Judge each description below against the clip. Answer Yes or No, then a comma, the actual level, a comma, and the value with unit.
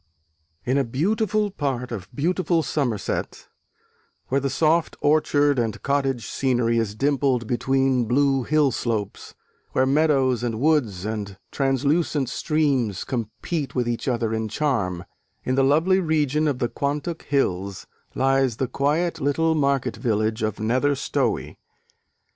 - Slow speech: Yes, slow, 130 wpm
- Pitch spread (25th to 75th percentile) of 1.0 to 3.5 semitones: No, average, 4.0 semitones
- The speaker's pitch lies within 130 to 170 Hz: Yes, low, 135 Hz